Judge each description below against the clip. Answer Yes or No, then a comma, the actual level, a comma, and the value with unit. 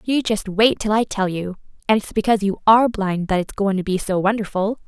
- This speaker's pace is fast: Yes, fast, 245 wpm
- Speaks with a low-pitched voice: No, high, 205 Hz